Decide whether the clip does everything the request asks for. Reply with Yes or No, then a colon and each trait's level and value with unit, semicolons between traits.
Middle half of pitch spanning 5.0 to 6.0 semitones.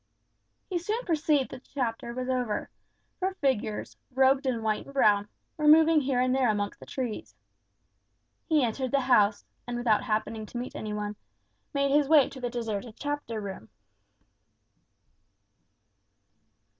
No: average, 4.4 semitones